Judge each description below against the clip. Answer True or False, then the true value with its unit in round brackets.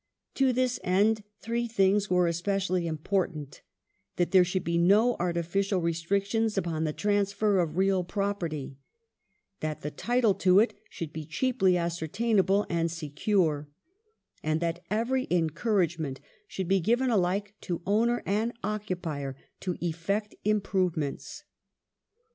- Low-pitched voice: False (185 Hz)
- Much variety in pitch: False (3.7 semitones)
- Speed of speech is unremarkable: False (130 wpm)